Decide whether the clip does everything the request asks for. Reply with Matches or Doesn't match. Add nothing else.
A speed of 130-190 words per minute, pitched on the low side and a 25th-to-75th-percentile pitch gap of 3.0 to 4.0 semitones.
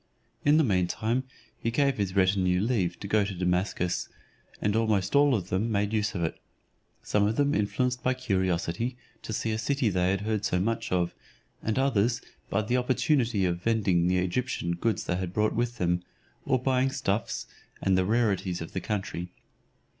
Doesn't match